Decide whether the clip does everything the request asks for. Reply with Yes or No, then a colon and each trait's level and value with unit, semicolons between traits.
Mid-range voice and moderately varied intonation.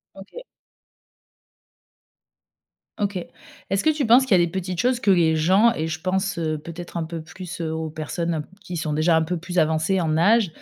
Yes: medium, 175 Hz; average, 3.3 semitones